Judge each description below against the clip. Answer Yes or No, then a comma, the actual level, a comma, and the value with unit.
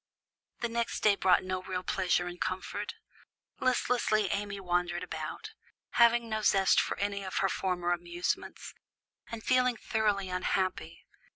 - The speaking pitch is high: Yes, high, 195 Hz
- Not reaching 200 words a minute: Yes, slow, 135 wpm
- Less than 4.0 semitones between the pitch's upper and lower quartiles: Yes, average, 3.2 semitones